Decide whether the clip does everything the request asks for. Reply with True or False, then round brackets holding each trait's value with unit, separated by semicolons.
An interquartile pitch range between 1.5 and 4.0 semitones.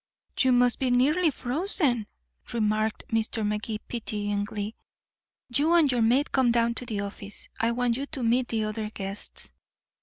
True (3.3 semitones)